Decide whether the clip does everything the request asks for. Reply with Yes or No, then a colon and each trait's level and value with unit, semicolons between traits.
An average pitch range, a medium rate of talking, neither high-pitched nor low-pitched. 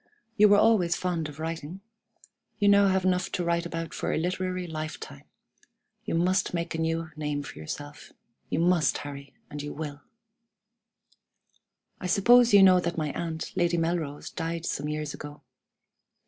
Yes: average, 3.2 semitones; average, 160 wpm; medium, 170 Hz